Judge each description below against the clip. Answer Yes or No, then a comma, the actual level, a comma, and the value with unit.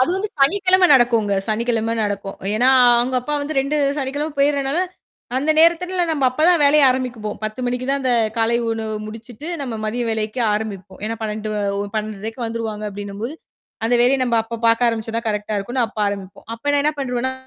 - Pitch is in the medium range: No, high, 240 Hz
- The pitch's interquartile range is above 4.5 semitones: No, average, 4.2 semitones